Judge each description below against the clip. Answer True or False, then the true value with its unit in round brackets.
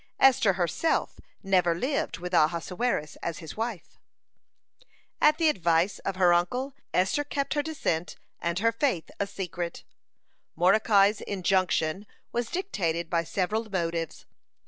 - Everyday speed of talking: False (130 wpm)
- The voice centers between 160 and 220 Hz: True (190 Hz)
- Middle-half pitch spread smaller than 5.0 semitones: False (5.4 semitones)